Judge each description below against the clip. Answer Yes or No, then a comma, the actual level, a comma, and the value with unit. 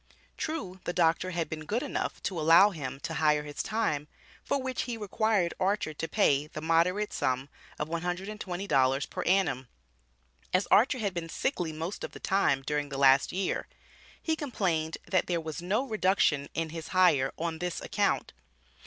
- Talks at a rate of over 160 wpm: Yes, average, 170 wpm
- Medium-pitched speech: Yes, medium, 170 Hz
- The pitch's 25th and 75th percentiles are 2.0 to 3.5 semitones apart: No, average, 4.3 semitones